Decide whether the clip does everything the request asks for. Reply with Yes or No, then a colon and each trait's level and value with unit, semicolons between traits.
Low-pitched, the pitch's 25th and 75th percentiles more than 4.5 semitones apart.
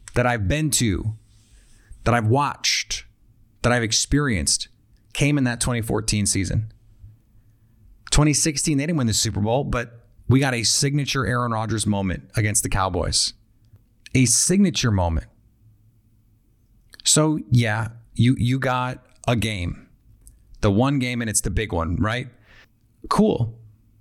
No: low, 110 Hz; narrow, 2.4 semitones